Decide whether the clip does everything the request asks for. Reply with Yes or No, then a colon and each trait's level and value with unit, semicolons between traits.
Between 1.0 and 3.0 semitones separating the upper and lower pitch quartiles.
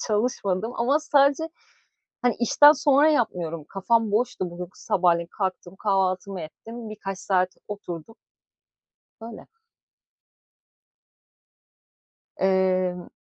No: average, 4.4 semitones